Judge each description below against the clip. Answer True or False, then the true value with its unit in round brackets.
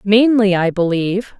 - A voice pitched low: False (200 Hz)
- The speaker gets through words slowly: True (130 wpm)